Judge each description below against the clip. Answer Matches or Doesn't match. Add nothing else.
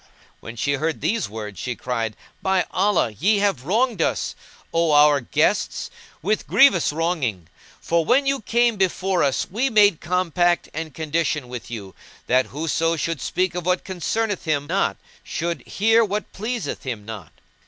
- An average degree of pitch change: Doesn't match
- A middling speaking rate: Matches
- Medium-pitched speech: Matches